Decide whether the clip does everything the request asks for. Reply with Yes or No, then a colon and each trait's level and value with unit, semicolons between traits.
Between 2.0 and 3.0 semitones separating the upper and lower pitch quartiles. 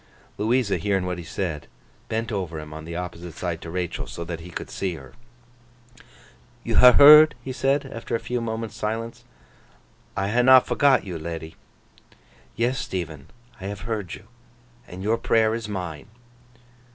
No: average, 5.2 semitones